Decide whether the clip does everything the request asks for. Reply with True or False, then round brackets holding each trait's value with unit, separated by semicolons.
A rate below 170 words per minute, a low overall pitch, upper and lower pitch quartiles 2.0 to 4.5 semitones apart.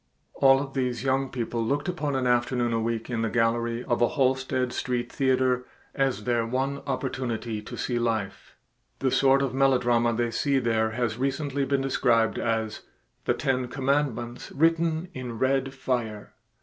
True (160 wpm; 125 Hz; 2.5 semitones)